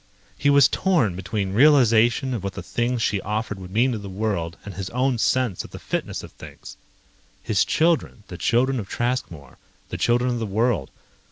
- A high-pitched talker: No, low, 115 Hz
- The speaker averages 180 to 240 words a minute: Yes, average, 190 wpm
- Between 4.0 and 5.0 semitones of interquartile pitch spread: Yes, average, 4.5 semitones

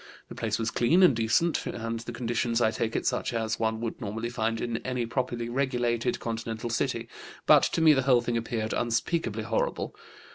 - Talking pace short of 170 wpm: No, average, 190 wpm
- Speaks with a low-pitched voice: Yes, low, 115 Hz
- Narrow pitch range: Yes, narrow, 1.4 semitones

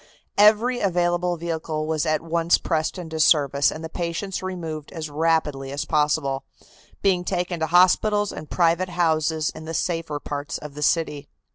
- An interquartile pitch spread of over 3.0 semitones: No, narrow, 2.5 semitones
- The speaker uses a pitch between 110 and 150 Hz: No, medium, 165 Hz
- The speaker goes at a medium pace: Yes, average, 160 wpm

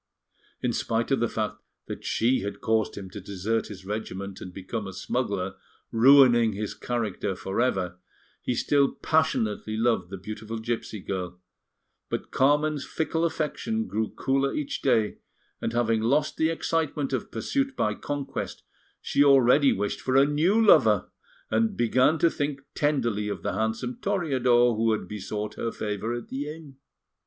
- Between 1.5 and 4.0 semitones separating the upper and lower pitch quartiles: No, average, 5.1 semitones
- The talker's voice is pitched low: Yes, low, 120 Hz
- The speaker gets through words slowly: No, average, 160 wpm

